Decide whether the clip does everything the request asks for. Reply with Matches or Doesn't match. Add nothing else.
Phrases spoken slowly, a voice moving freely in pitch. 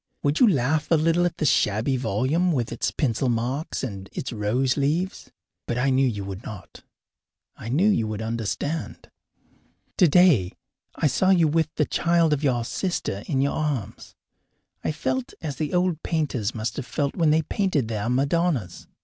Doesn't match